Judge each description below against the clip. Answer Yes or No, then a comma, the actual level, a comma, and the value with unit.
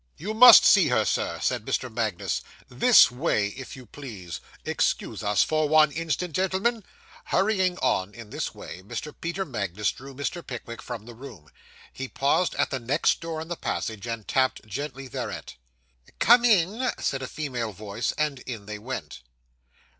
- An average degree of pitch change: No, wide, 7.0 semitones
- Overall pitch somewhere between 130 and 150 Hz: Yes, low, 135 Hz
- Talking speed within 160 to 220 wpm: Yes, average, 170 wpm